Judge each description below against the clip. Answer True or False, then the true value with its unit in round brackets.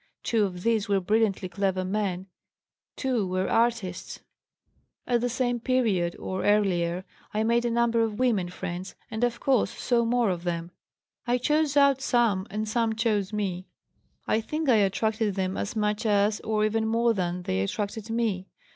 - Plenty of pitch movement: False (3.8 semitones)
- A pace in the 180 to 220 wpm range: False (170 wpm)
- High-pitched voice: True (215 Hz)